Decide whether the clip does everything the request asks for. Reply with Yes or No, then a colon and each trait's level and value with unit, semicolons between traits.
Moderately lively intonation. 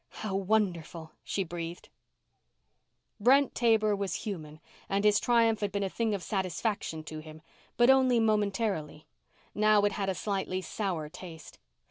Yes: average, 4.0 semitones